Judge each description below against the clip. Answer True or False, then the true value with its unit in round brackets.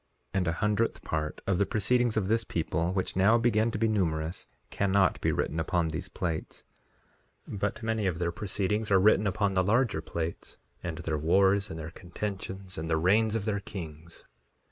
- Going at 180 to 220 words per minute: True (190 wpm)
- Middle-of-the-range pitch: False (95 Hz)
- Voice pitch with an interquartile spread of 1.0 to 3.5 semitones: False (3.9 semitones)